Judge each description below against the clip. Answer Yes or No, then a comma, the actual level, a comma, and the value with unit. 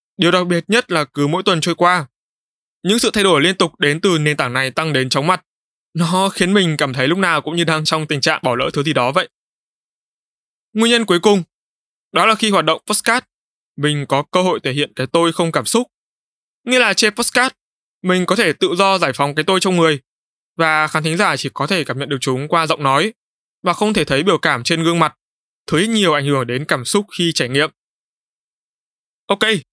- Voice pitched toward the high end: No, medium, 170 Hz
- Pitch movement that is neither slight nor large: Yes, average, 4.7 semitones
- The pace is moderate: Yes, average, 230 wpm